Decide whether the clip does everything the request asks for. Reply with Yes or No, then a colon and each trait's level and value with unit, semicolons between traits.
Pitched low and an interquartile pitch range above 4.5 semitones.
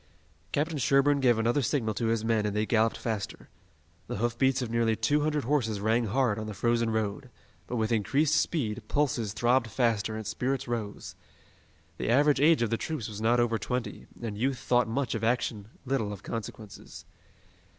No: low, 115 Hz; average, 3.3 semitones